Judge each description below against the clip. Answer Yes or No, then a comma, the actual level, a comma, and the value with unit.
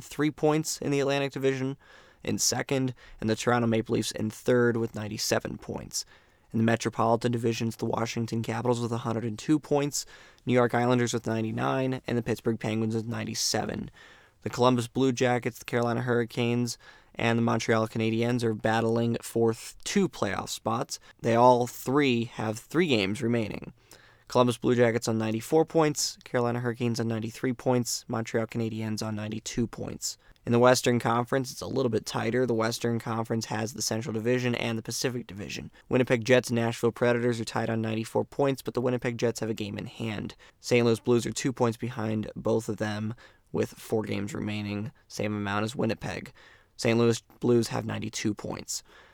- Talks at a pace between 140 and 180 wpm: Yes, average, 175 wpm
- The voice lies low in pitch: Yes, low, 115 Hz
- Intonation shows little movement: Yes, narrow, 1.8 semitones